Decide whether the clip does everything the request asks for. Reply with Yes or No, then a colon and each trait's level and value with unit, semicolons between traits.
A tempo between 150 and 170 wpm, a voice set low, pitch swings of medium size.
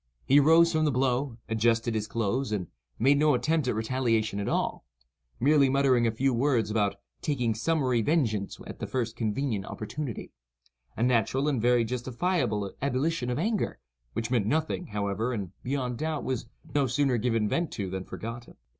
Yes: average, 165 wpm; low, 120 Hz; average, 4.3 semitones